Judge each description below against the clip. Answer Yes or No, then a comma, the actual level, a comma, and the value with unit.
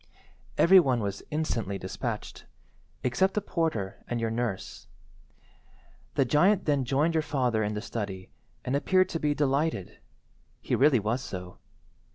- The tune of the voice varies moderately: No, wide, 6.2 semitones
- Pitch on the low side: Yes, low, 130 Hz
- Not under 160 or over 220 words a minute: No, average, 145 wpm